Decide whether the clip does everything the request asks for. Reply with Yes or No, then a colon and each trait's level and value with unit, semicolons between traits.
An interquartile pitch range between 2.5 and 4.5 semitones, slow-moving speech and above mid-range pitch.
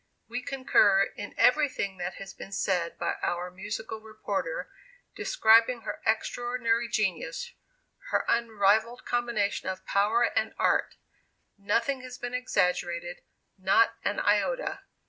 Yes: average, 3.7 semitones; slow, 120 wpm; high, 220 Hz